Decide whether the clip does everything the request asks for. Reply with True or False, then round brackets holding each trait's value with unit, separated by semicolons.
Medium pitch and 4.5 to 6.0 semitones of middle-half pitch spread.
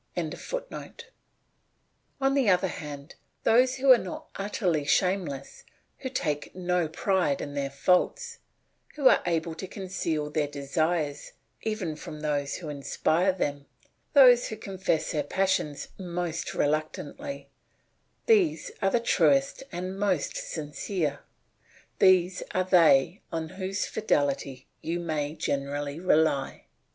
True (175 Hz; 4.8 semitones)